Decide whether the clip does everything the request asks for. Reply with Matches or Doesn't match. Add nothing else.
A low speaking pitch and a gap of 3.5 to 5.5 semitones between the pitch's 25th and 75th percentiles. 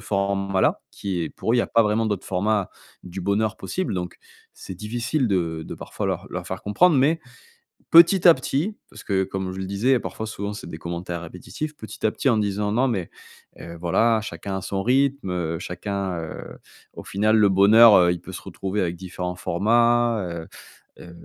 Matches